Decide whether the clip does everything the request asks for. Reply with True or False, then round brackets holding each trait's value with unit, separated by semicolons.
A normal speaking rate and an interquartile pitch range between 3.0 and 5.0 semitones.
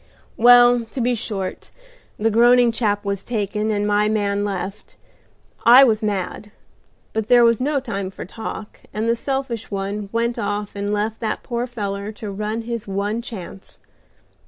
False (160 wpm; 2.6 semitones)